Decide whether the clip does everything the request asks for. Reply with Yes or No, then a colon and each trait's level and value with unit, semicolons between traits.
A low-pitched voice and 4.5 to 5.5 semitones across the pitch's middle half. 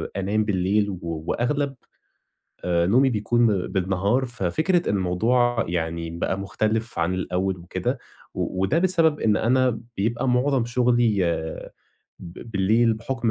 Yes: low, 110 Hz; average, 4.8 semitones